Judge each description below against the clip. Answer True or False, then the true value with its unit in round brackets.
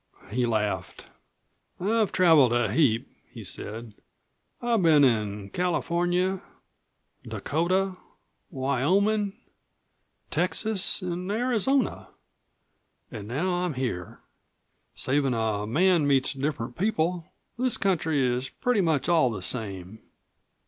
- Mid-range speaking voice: True (155 Hz)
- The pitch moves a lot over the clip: True (7.6 semitones)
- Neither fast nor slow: False (100 wpm)